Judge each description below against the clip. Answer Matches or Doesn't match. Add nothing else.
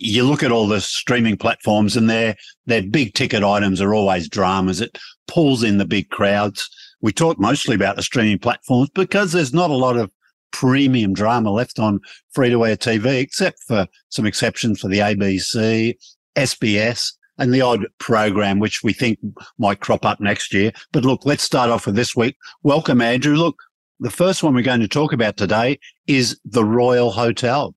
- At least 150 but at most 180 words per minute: Doesn't match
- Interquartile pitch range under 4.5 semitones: Matches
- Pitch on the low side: Matches